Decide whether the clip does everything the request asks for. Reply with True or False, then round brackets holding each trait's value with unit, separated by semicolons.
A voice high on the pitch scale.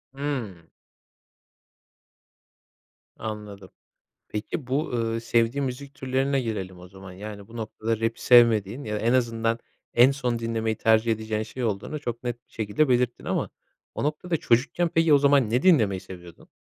False (115 Hz)